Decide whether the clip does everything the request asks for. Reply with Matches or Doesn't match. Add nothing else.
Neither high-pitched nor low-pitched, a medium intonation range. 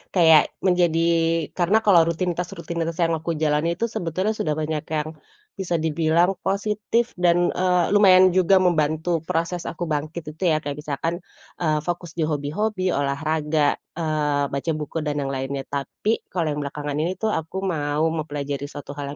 Matches